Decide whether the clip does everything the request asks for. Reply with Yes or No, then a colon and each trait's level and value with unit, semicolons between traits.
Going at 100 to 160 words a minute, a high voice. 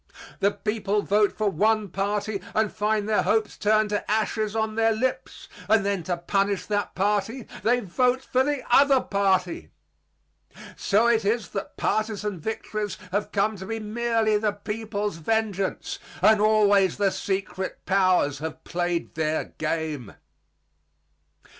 Yes: average, 140 wpm; high, 210 Hz